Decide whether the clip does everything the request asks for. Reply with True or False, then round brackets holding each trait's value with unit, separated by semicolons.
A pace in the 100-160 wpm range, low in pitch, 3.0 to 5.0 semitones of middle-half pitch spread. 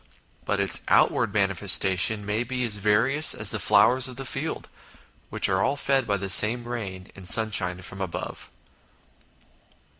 True (155 wpm; 105 Hz; 4.0 semitones)